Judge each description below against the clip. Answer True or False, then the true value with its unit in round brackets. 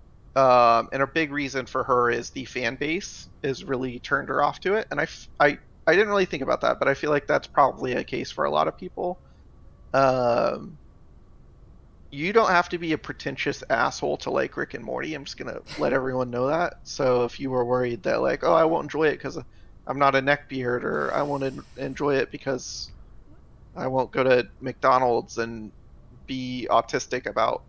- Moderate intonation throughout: False (2.2 semitones)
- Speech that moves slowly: False (205 wpm)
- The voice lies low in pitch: True (130 Hz)